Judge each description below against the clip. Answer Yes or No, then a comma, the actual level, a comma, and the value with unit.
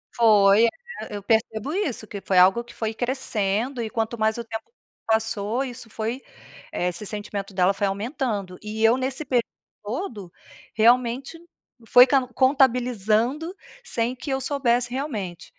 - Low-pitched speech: No, high, 230 Hz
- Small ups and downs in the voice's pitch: No, average, 3.5 semitones